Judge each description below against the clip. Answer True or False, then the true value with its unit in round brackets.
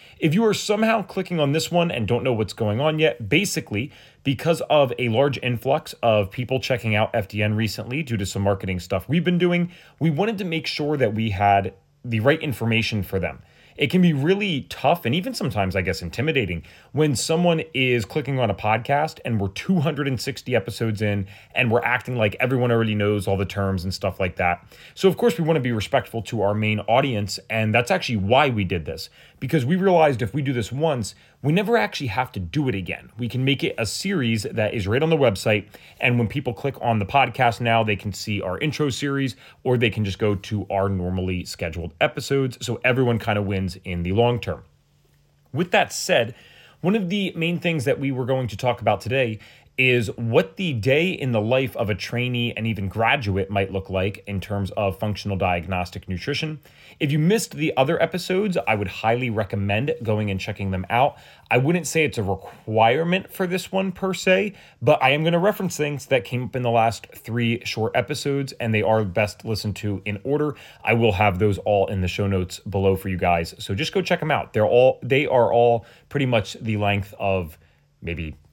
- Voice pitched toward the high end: False (120 Hz)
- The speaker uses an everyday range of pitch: False (6.4 semitones)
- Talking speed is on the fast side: True (215 wpm)